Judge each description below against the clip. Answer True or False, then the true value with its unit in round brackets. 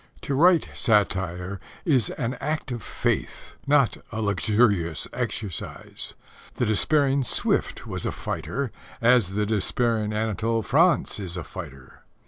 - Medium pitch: False (110 Hz)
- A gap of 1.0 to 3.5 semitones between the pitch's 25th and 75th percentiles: False (5.0 semitones)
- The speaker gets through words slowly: True (125 wpm)